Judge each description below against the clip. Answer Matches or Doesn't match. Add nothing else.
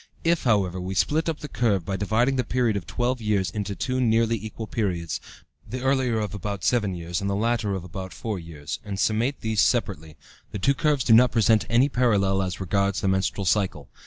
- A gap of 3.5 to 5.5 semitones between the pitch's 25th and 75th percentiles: Matches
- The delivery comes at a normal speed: Doesn't match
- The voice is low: Matches